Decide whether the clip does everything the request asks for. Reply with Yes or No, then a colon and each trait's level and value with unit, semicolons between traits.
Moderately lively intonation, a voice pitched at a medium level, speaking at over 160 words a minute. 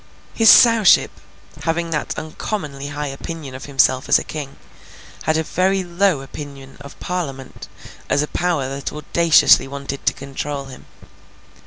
No: average, 3.8 semitones; medium, 145 Hz; average, 145 wpm